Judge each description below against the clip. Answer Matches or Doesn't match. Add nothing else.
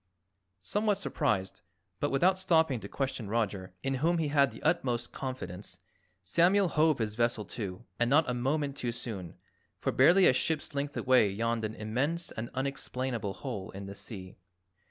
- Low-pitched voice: Matches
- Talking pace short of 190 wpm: Matches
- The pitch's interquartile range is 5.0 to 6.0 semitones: Matches